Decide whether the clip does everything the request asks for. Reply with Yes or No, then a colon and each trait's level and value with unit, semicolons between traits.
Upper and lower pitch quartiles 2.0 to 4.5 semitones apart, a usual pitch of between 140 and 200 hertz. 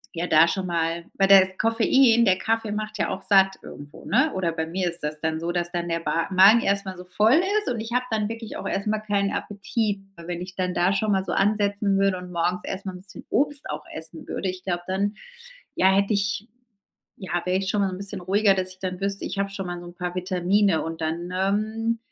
Yes: average, 2.7 semitones; high, 190 Hz